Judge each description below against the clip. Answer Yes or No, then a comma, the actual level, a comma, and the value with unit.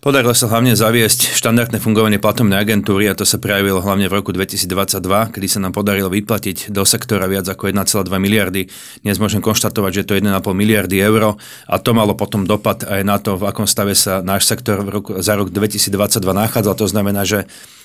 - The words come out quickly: Yes, fast, 200 wpm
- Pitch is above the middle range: No, low, 100 Hz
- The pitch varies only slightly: Yes, narrow, 1.7 semitones